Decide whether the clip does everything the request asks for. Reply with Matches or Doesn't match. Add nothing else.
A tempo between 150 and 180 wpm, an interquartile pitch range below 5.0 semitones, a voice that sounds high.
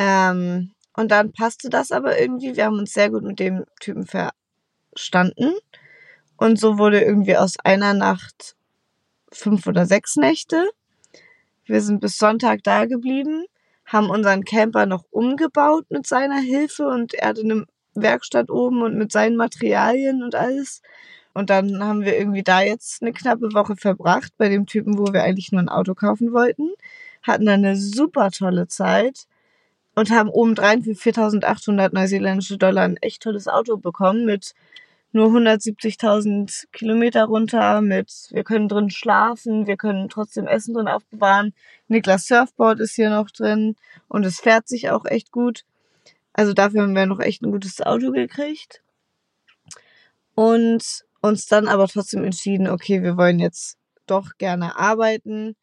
Matches